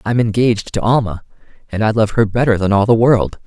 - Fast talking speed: Yes, fast, 225 wpm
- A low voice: Yes, low, 110 Hz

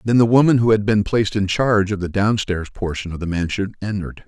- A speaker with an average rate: No, fast, 240 wpm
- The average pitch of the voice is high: No, low, 105 Hz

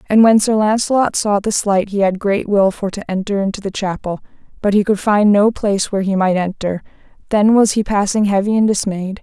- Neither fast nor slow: No, fast, 220 wpm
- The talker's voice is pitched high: Yes, high, 205 Hz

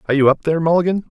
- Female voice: No, male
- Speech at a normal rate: No, fast, 260 wpm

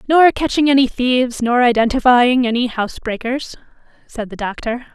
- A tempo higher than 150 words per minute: No, average, 145 wpm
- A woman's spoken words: Yes, female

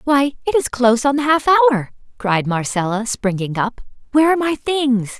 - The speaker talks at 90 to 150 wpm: No, average, 185 wpm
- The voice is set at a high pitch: Yes, very high, 255 Hz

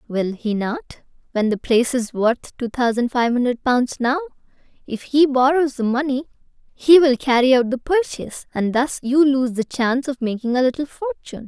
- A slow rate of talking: No, average, 185 wpm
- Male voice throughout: No, female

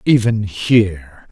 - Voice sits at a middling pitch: No, low, 100 Hz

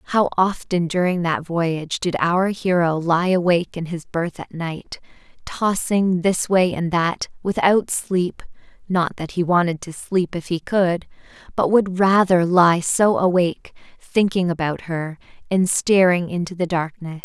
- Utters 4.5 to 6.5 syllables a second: No, 4.1 syllables/s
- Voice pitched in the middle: Yes, medium, 175 Hz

